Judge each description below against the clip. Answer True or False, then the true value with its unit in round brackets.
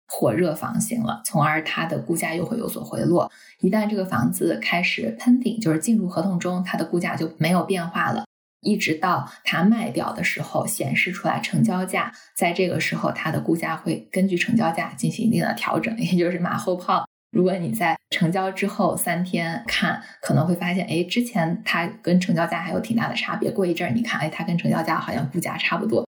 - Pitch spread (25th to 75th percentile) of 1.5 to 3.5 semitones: True (3.1 semitones)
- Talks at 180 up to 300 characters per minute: False (320 characters per minute)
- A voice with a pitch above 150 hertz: True (185 Hz)